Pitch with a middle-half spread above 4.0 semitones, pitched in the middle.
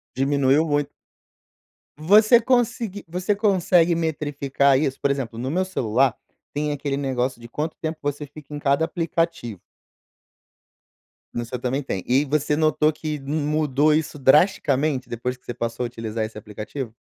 No: average, 3.5 semitones; medium, 145 Hz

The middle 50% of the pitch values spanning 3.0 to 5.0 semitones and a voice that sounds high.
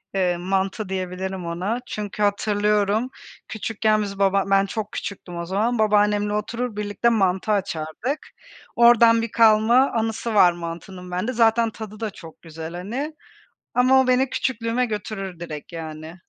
Yes: average, 3.7 semitones; high, 205 Hz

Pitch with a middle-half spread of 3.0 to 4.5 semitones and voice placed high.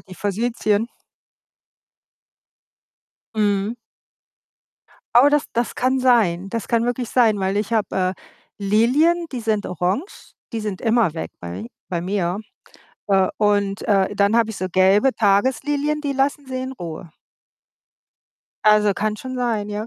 Yes: average, 3.9 semitones; high, 215 Hz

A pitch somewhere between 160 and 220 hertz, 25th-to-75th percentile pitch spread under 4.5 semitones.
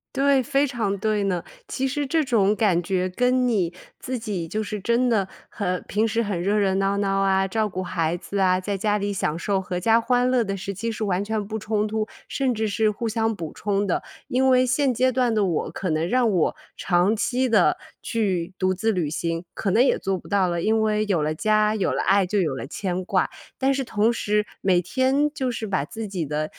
Yes: high, 210 Hz; average, 3.7 semitones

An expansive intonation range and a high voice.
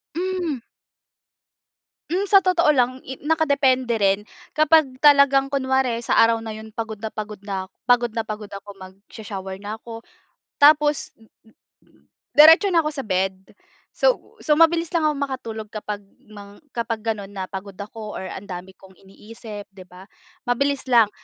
Yes: wide, 5.7 semitones; high, 225 Hz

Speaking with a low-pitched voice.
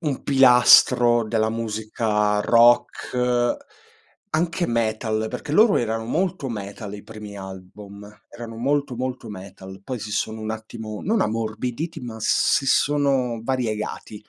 Yes: low, 115 Hz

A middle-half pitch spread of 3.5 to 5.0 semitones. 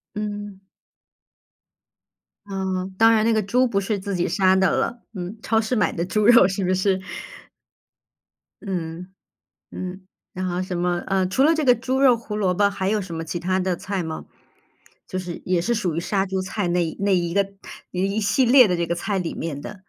No: average, 2.9 semitones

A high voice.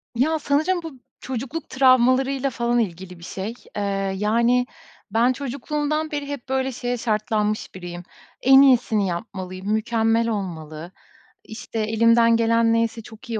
Yes: high, 230 Hz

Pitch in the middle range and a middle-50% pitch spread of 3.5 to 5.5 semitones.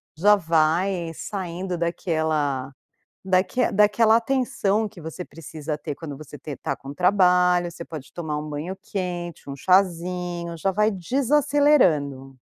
Yes: medium, 175 Hz; average, 3.9 semitones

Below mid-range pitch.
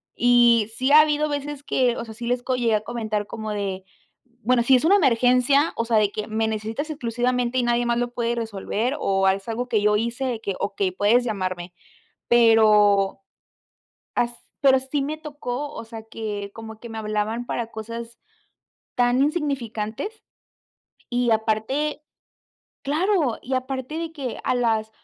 No: high, 235 Hz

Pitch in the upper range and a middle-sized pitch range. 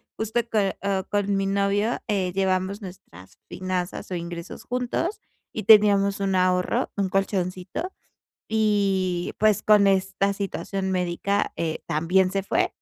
No: high, 195 Hz; narrow, 1.8 semitones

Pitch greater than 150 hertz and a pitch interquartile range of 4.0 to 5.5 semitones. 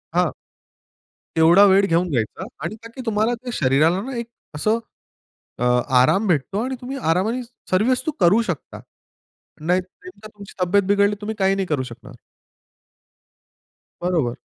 Yes: high, 190 Hz; average, 4.5 semitones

